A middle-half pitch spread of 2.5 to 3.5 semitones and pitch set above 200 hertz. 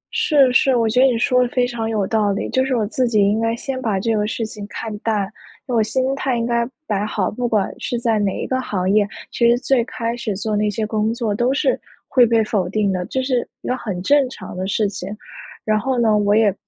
Yes: average, 3.0 semitones; high, 225 Hz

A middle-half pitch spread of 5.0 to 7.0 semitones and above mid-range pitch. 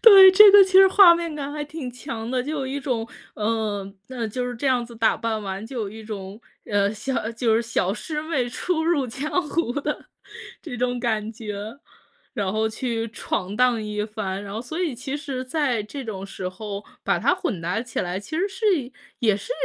Yes: average, 5.3 semitones; high, 235 Hz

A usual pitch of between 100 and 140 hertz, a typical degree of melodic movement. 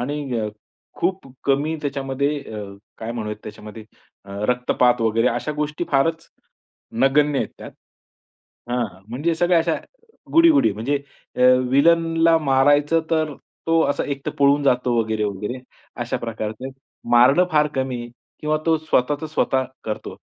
Yes: low, 135 Hz; average, 4.3 semitones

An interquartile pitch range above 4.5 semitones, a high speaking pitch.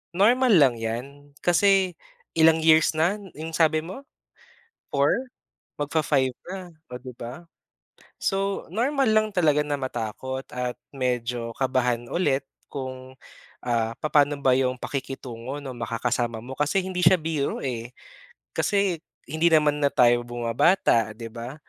No: average, 5.1 semitones; medium, 140 Hz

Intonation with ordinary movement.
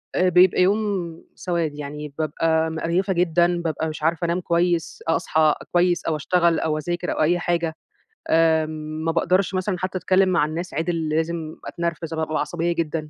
No: narrow, 1.8 semitones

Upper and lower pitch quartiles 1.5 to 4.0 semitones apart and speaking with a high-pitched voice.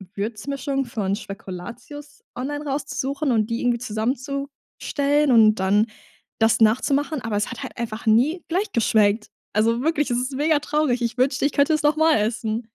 No: average, 4.7 semitones; very high, 250 Hz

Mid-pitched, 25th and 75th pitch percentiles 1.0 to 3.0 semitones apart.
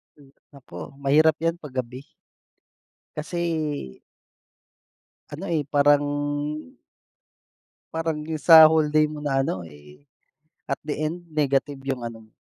Yes: medium, 145 Hz; average, 2.7 semitones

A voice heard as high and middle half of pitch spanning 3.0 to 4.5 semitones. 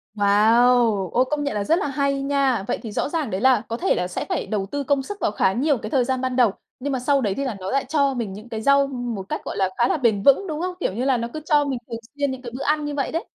Yes: very high, 260 Hz; average, 4.0 semitones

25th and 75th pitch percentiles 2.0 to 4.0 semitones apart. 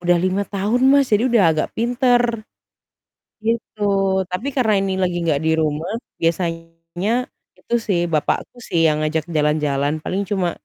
No: wide, 5.5 semitones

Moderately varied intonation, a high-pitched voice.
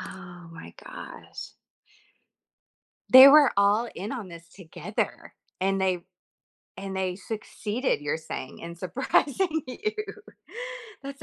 No: wide, 6.7 semitones; high, 195 Hz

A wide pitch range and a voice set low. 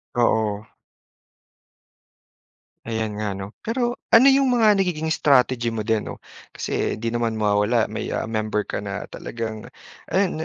Yes: wide, 6.9 semitones; low, 115 Hz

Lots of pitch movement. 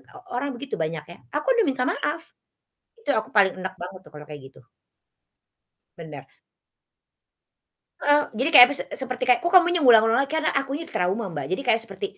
Yes: wide, 7.7 semitones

